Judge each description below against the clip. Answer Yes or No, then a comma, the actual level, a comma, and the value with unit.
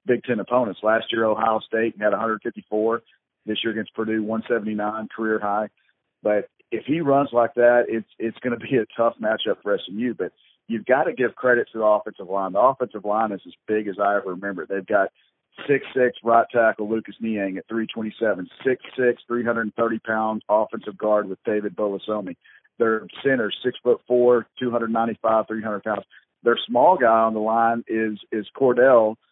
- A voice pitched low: Yes, low, 110 Hz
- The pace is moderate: Yes, average, 195 wpm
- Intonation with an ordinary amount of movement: No, narrow, 1.7 semitones